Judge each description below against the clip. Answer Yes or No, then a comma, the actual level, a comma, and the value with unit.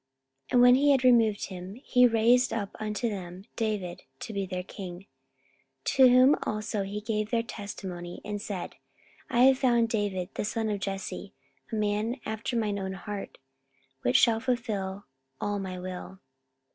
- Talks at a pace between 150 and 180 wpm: Yes, average, 165 wpm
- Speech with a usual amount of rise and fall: Yes, average, 3.1 semitones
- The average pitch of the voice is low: No, high, 210 Hz